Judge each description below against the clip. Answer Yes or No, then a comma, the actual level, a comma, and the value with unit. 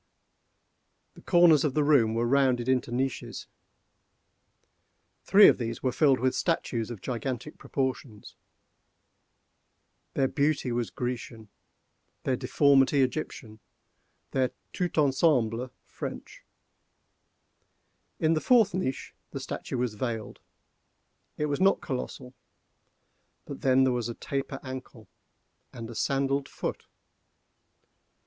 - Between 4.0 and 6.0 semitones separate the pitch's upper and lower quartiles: No, average, 3.0 semitones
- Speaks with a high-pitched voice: No, low, 130 Hz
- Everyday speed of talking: No, slow, 110 wpm